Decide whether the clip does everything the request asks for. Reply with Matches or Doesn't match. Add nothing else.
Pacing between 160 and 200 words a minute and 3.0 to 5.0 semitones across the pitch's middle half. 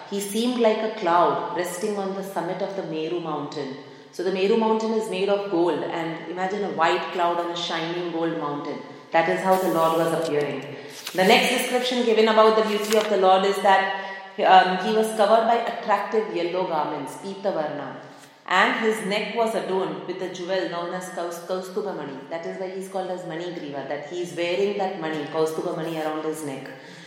Matches